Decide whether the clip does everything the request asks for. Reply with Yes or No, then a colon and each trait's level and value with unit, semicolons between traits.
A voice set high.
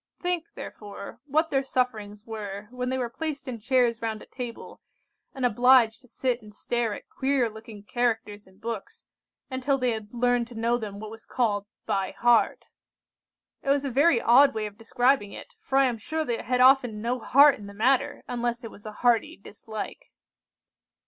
Yes: high, 240 Hz